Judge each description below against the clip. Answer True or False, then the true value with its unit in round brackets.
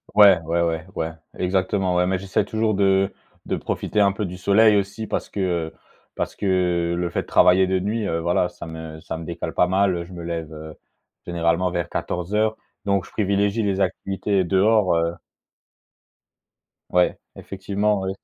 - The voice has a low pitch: True (95 Hz)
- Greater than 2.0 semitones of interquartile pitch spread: True (2.6 semitones)